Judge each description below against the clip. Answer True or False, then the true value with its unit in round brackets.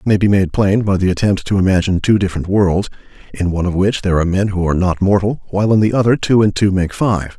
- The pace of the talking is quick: True (270 wpm)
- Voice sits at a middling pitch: False (95 Hz)